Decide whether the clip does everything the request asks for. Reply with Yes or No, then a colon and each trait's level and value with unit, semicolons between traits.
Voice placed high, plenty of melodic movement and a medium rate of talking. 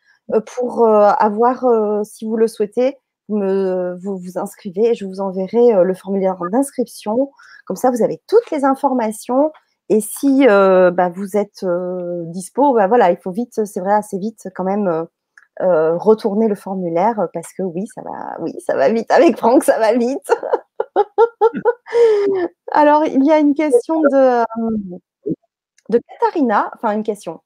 Yes: high, 225 Hz; wide, 6.2 semitones; average, 165 wpm